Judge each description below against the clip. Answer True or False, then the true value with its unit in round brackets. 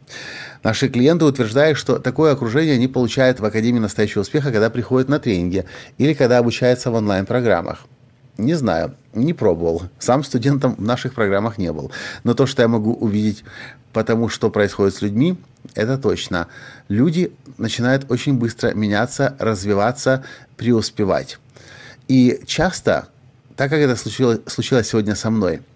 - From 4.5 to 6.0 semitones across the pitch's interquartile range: False (3.3 semitones)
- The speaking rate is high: False (145 wpm)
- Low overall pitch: True (120 Hz)